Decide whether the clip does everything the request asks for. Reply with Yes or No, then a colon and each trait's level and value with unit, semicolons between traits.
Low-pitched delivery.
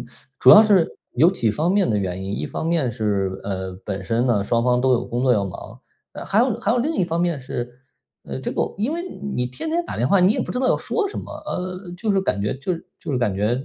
Yes: low, 130 Hz